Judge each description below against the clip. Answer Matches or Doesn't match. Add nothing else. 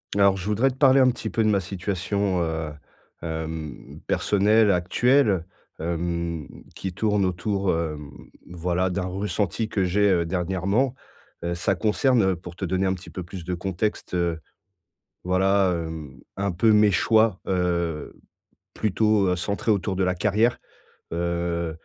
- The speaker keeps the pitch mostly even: Doesn't match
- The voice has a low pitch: Matches